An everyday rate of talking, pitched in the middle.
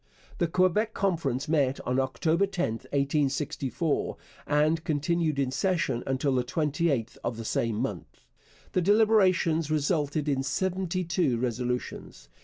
No: slow, 125 wpm; medium, 150 Hz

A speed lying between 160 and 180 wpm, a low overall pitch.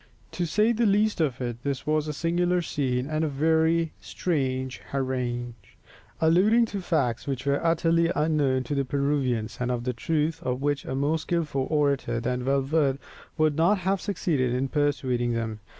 No: average, 170 wpm; medium, 145 Hz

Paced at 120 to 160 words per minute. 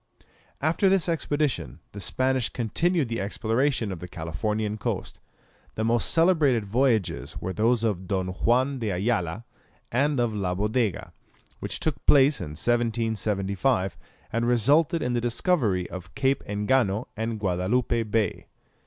Yes: slow, 135 wpm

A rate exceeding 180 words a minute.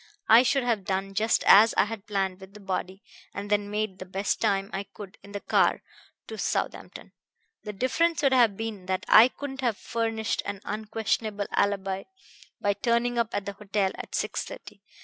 Yes: average, 190 wpm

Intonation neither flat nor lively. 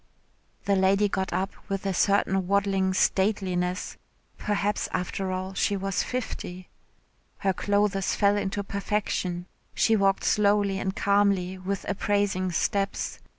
No: narrow, 1.2 semitones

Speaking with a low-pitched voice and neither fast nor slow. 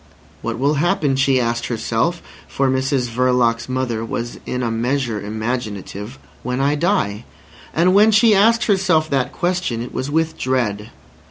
Yes: low, 130 Hz; average, 155 wpm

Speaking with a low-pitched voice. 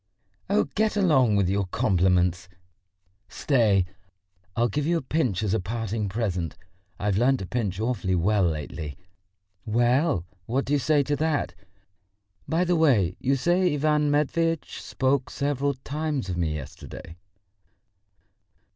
Yes: low, 120 Hz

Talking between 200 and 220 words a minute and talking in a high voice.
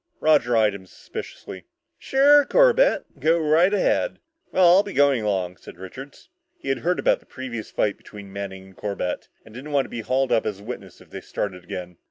No: fast, 205 wpm; low, 120 Hz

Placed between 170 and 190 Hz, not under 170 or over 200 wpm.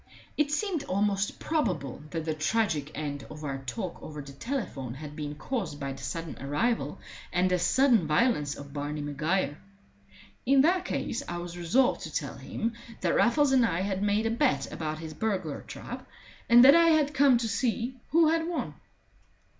Yes: medium, 185 Hz; average, 180 wpm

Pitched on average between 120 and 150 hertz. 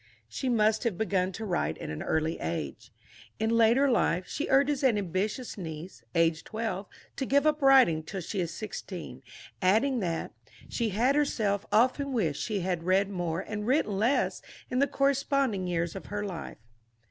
No: high, 205 Hz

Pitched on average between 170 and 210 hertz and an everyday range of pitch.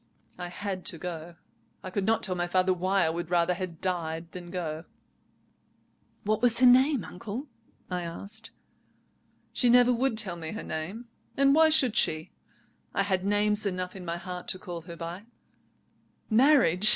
Yes: medium, 185 Hz; average, 4.1 semitones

